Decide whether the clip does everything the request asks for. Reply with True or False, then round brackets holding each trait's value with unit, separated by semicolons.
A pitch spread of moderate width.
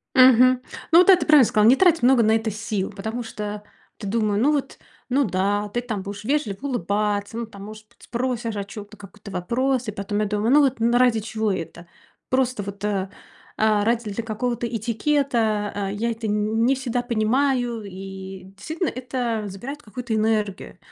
True (3.3 semitones)